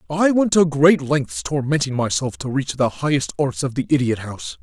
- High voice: No, medium, 140 Hz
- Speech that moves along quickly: Yes, fast, 210 wpm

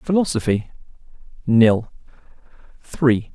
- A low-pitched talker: Yes, low, 125 Hz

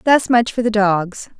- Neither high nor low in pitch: No, high, 215 Hz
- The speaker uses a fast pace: Yes, fast, 215 wpm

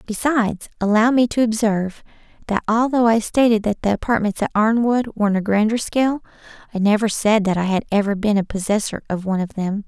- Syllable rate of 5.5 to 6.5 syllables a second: Yes, 6.0 syllables/s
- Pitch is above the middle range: Yes, high, 215 Hz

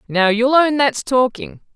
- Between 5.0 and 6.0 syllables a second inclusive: No, 4.1 syllables/s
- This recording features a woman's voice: Yes, female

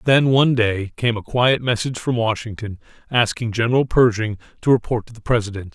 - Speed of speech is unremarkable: Yes, average, 180 wpm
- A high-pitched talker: No, low, 115 Hz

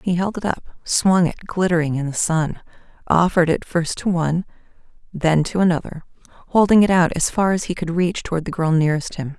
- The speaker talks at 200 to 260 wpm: Yes, fast, 205 wpm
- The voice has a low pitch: No, medium, 170 Hz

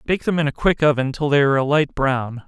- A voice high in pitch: No, medium, 145 Hz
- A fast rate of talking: Yes, fast, 290 wpm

